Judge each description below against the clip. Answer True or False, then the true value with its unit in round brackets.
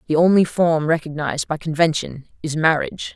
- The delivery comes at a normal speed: True (150 wpm)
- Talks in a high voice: False (160 Hz)